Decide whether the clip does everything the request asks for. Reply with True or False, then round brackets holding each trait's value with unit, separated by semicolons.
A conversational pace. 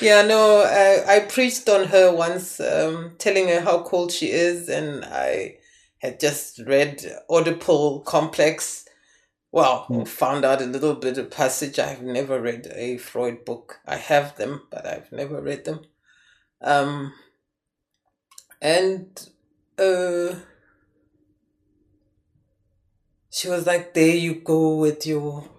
False (130 wpm)